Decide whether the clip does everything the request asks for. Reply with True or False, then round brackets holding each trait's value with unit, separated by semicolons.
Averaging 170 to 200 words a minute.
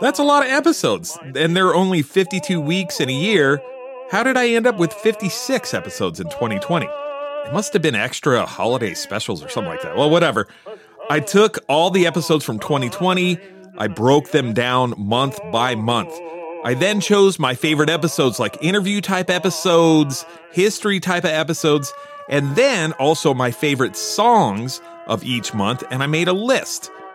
True (175 wpm)